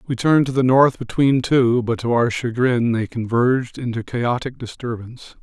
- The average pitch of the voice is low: Yes, low, 120 Hz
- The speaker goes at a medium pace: Yes, average, 175 wpm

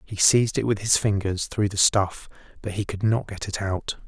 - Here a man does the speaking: Yes, male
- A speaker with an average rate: No, fast, 235 wpm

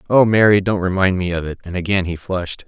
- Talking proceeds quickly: Yes, fast, 245 wpm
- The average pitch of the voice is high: No, very low, 95 Hz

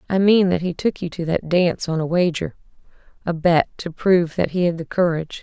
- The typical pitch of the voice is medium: Yes, medium, 170 Hz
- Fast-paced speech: Yes, fast, 210 wpm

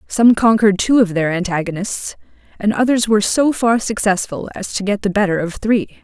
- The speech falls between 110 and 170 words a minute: No, average, 190 wpm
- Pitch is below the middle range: No, high, 205 Hz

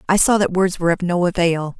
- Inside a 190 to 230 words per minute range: No, fast, 265 wpm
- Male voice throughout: No, female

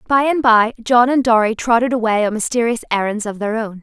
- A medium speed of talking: No, fast, 220 wpm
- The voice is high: Yes, high, 230 Hz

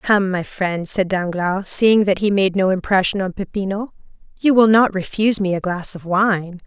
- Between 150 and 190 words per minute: No, average, 200 wpm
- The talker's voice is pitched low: No, high, 195 Hz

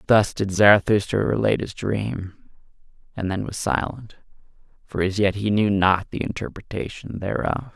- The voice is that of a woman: No, male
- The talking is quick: No, average, 145 wpm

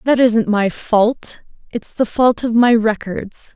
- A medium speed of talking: Yes, average, 170 wpm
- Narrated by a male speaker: No, female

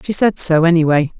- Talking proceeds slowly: No, average, 200 wpm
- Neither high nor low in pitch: Yes, medium, 170 Hz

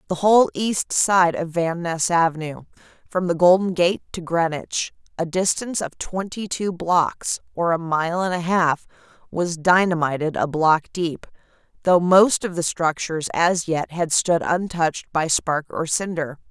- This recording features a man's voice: No, female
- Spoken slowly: No, average, 165 wpm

